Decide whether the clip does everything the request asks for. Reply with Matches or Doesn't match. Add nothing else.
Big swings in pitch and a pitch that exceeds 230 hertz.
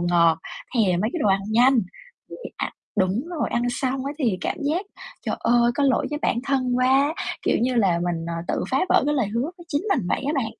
Matches